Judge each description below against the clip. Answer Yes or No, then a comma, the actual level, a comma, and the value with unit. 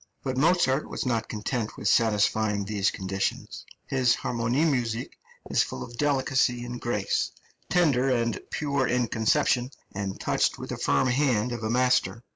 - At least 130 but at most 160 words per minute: Yes, average, 155 wpm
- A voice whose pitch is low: Yes, low, 120 Hz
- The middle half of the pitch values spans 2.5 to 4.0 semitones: Yes, average, 3.2 semitones